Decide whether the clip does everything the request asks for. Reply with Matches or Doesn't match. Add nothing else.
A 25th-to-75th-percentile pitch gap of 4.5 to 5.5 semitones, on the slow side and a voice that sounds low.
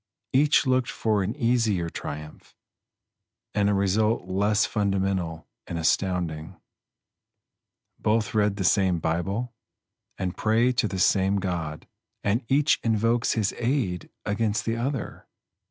Doesn't match